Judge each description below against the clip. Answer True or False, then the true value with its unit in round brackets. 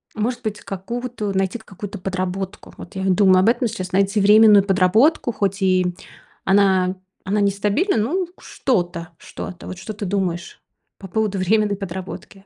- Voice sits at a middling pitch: False (195 Hz)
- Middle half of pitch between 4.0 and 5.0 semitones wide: False (2.5 semitones)